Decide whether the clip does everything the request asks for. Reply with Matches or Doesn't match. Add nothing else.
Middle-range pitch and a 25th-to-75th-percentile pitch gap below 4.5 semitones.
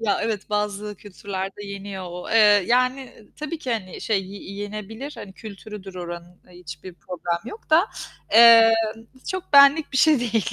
Doesn't match